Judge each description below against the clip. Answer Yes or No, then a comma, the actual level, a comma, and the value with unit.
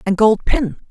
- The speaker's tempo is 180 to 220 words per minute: Yes, average, 200 wpm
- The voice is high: Yes, high, 205 Hz